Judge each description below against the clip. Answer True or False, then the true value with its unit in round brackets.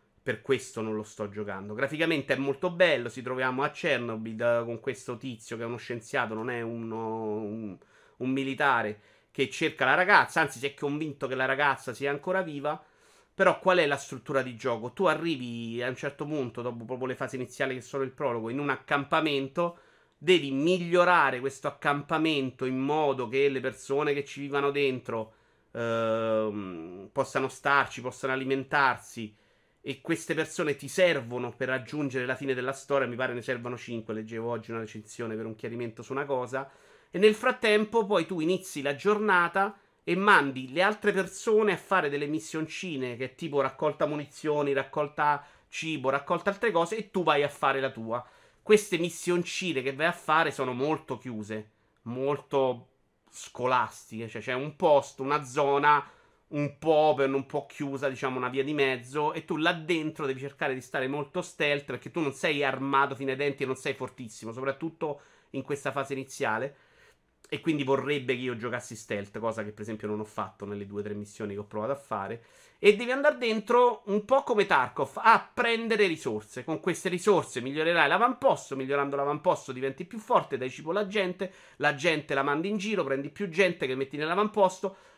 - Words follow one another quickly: True (185 wpm)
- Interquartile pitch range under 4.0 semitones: False (4.3 semitones)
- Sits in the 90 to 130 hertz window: False (140 Hz)